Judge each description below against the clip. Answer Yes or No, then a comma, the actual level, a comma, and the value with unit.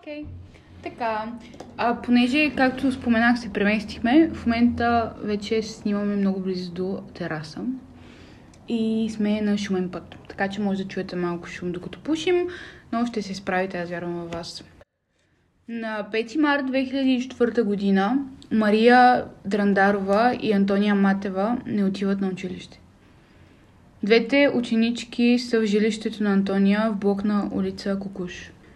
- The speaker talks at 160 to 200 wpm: No, average, 135 wpm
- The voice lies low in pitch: No, high, 215 Hz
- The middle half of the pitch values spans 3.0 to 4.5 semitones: Yes, average, 3.5 semitones